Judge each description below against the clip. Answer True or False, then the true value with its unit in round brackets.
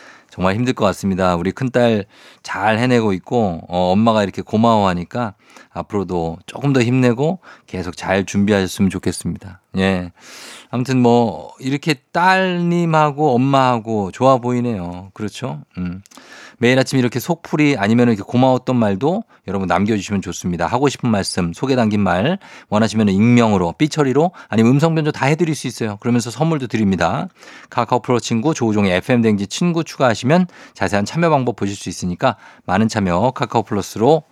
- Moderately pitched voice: False (115 Hz)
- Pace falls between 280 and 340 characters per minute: False (365 characters per minute)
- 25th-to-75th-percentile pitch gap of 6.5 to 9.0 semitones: False (5.2 semitones)